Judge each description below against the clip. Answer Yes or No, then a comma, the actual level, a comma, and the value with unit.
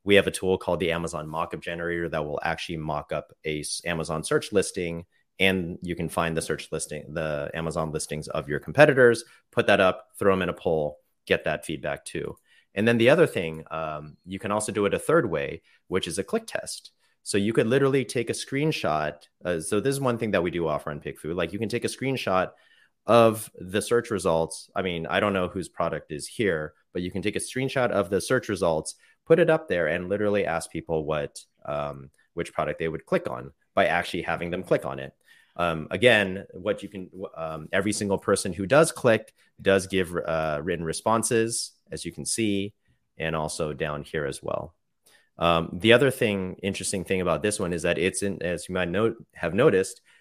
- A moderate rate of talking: No, fast, 215 wpm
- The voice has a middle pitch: No, very low, 95 Hz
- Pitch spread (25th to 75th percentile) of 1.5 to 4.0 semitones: No, average, 4.5 semitones